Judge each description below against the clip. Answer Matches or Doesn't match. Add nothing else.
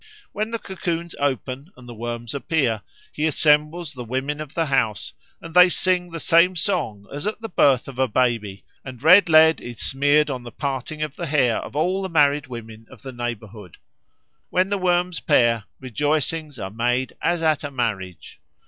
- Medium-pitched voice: Matches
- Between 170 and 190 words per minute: Matches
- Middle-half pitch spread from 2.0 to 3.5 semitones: Doesn't match